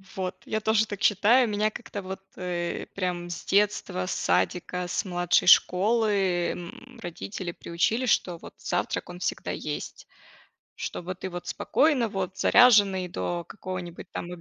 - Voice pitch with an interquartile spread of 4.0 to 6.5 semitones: No, average, 3.0 semitones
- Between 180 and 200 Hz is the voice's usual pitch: Yes, medium, 185 Hz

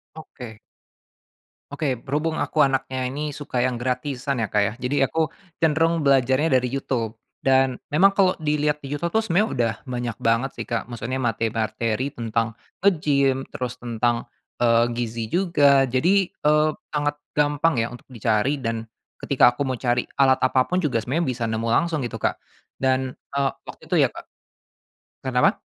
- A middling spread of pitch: Yes, average, 3.7 semitones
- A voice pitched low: Yes, low, 130 Hz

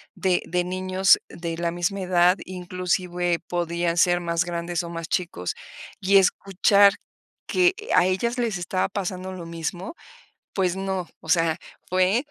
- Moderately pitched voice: Yes, medium, 180 Hz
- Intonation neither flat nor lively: No, narrow, 1.7 semitones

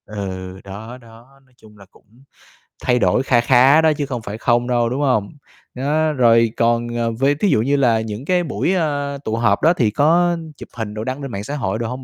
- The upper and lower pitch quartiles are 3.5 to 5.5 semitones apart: Yes, average, 4.1 semitones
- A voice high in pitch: No, low, 120 Hz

